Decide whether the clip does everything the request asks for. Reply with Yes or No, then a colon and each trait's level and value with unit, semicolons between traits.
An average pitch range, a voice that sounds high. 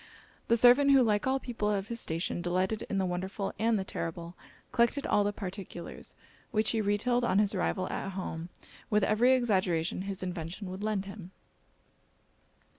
Yes: average, 3.3 semitones; high, 200 Hz